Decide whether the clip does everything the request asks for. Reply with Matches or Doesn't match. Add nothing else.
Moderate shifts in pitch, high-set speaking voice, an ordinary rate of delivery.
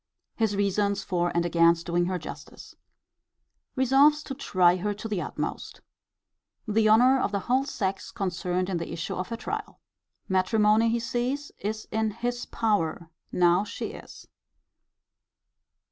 Matches